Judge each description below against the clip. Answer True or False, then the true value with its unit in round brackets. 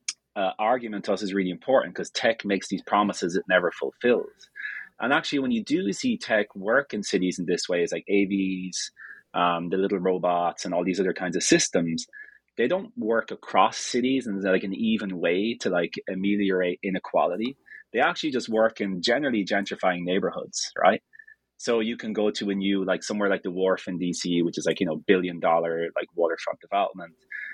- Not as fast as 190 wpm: False (195 wpm)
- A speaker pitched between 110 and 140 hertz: False (100 Hz)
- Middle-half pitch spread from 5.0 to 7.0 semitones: True (5.5 semitones)